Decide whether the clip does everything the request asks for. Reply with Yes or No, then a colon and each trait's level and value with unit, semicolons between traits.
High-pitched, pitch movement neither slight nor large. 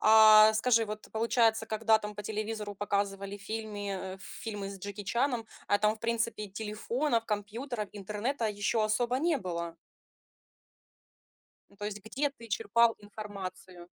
No: high, 215 Hz; narrow, 1.9 semitones